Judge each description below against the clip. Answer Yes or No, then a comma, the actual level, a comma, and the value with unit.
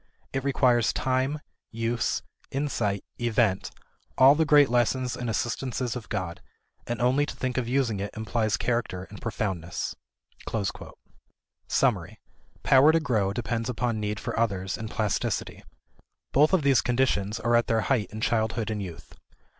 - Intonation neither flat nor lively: Yes, average, 3.3 semitones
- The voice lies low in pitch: Yes, low, 120 Hz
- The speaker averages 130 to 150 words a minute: Yes, average, 145 wpm